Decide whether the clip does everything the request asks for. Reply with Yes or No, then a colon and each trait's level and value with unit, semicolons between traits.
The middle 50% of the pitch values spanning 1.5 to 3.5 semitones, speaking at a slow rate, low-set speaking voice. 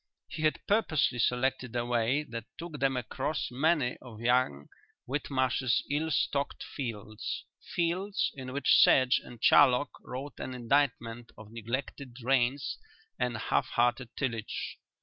Yes: average, 3.0 semitones; slow, 130 wpm; low, 130 Hz